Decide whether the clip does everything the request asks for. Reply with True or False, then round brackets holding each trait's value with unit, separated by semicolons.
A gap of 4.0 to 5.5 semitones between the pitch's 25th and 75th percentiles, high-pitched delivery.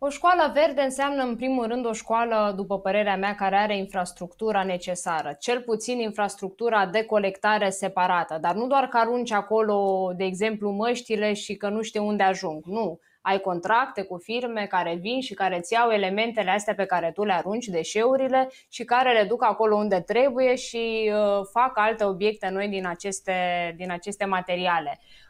False (3.3 semitones; 210 Hz)